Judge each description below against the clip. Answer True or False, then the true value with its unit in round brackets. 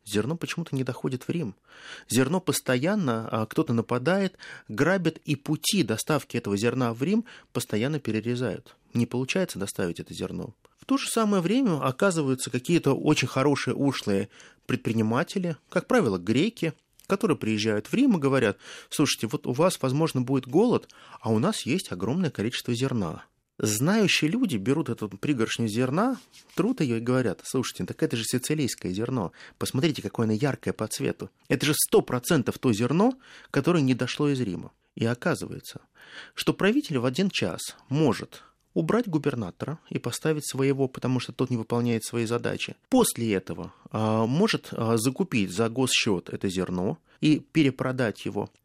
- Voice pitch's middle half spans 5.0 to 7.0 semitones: True (5.5 semitones)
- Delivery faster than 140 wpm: True (155 wpm)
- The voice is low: True (130 Hz)